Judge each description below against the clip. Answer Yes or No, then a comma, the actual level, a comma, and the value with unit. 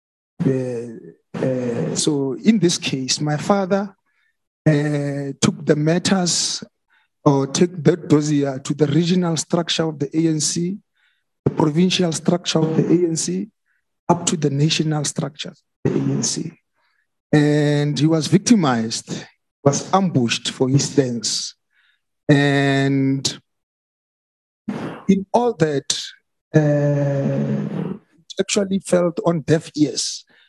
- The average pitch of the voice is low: No, medium, 155 Hz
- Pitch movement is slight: No, average, 3.9 semitones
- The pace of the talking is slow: Yes, slow, 115 wpm